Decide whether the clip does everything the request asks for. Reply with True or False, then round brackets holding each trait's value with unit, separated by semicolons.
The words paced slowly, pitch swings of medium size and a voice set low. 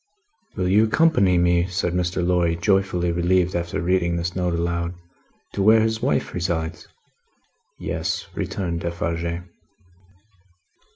False (120 wpm; 1.6 semitones; 90 Hz)